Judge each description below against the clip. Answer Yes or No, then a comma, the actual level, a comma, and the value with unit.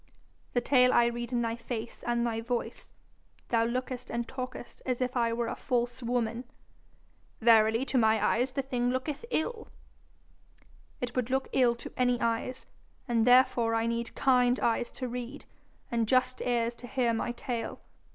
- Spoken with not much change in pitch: Yes, narrow, 1.5 semitones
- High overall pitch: Yes, high, 240 Hz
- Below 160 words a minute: No, average, 170 wpm